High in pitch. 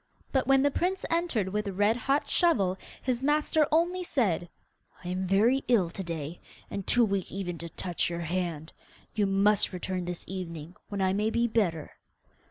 Yes: high, 200 Hz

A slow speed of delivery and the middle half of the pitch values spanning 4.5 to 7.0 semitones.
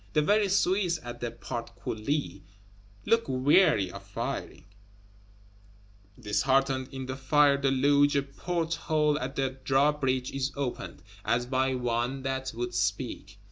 No: slow, 130 wpm; average, 3.3 semitones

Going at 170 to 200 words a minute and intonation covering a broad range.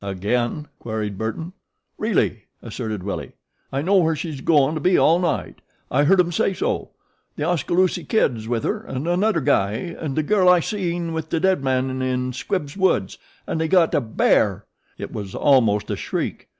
Yes: average, 180 wpm; wide, 6.6 semitones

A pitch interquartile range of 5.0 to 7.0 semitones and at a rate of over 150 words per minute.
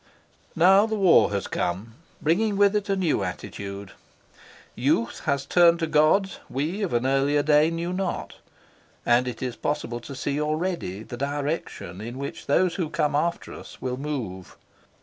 Yes: wide, 5.6 semitones; average, 165 wpm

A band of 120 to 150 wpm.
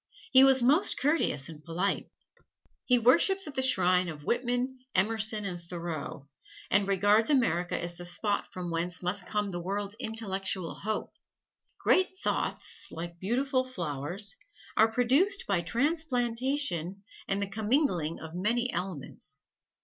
Yes: slow, 135 wpm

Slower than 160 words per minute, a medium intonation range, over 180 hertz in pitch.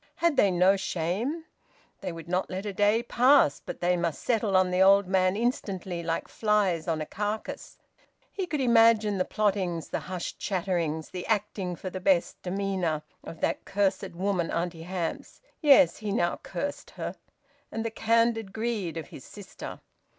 No: average, 170 wpm; average, 3.7 semitones; high, 190 Hz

